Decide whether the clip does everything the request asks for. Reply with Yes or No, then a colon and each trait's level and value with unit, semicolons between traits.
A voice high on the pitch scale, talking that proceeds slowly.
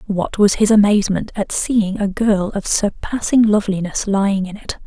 No: high, 200 Hz; average, 175 wpm